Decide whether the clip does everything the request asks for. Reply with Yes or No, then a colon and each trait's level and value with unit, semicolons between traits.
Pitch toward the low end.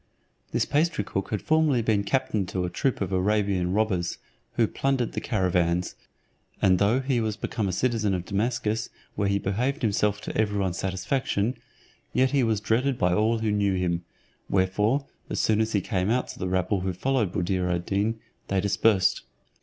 Yes: low, 105 Hz